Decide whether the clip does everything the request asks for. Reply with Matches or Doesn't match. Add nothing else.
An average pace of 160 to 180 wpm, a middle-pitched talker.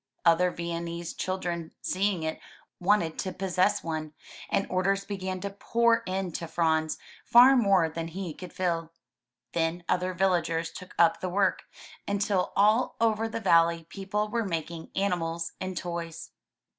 Doesn't match